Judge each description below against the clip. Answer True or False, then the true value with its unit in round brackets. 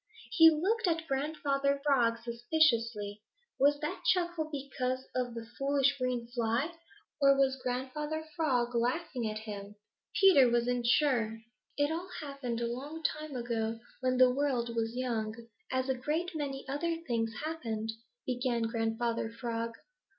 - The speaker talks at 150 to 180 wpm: False (140 wpm)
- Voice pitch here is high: True (255 Hz)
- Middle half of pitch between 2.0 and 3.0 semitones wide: False (3.9 semitones)